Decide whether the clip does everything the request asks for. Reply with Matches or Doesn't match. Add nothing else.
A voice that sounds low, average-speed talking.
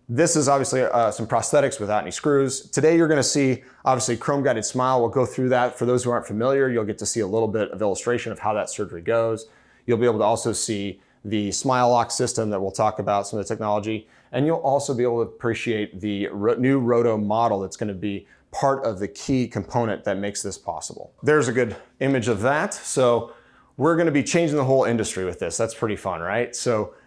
Doesn't match